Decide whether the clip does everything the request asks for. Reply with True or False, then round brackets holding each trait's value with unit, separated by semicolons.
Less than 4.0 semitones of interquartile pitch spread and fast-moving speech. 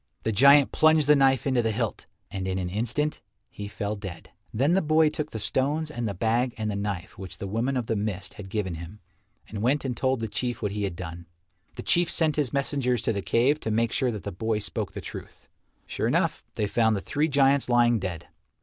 False (5.3 semitones; 230 wpm)